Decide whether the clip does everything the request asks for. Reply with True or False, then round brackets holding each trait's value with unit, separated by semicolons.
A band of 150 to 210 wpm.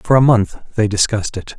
False (225 wpm)